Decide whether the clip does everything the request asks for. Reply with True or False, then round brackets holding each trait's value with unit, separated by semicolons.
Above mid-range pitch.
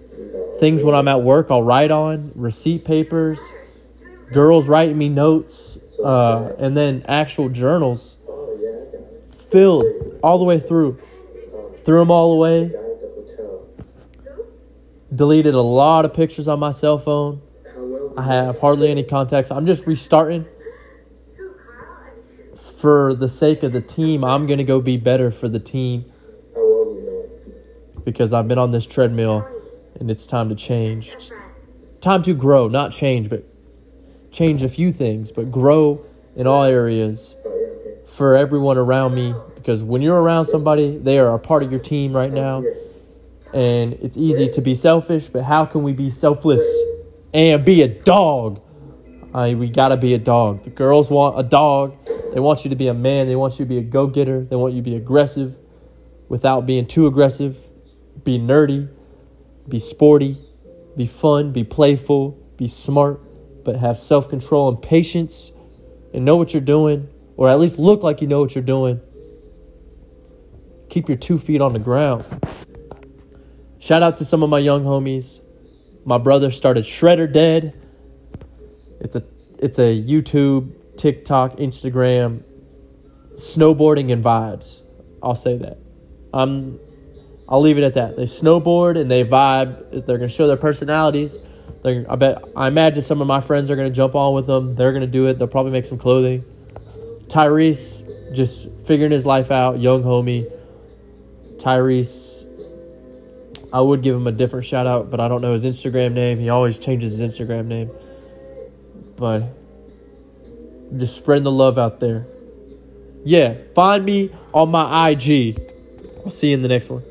False (135 Hz)